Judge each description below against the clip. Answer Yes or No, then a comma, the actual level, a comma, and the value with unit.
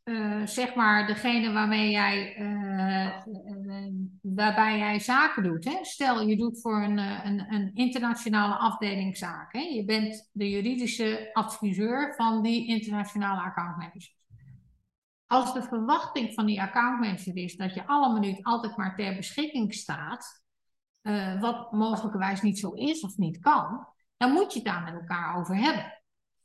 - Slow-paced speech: No, average, 160 wpm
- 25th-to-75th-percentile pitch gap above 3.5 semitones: No, average, 3.1 semitones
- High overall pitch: Yes, high, 210 Hz